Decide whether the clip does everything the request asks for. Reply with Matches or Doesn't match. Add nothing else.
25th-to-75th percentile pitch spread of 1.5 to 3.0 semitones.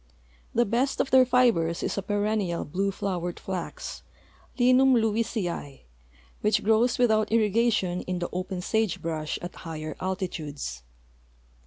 Doesn't match